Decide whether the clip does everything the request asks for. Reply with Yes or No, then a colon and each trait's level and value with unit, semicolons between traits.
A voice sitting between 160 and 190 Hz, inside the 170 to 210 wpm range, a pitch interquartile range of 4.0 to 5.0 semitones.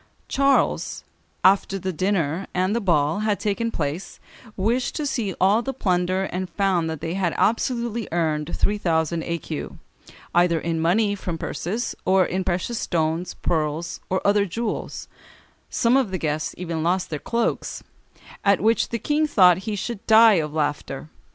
No: medium, 185 Hz; average, 160 wpm; average, 4.5 semitones